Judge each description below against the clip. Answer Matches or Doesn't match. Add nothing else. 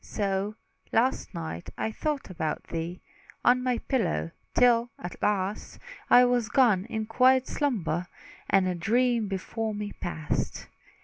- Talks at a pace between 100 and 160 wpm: Matches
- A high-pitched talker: Matches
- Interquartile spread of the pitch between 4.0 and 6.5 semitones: Matches